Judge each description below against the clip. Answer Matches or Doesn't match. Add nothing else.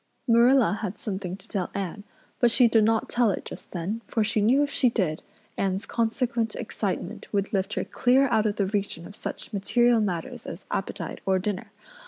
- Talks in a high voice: Matches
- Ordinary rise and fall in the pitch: Matches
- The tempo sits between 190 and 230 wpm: Matches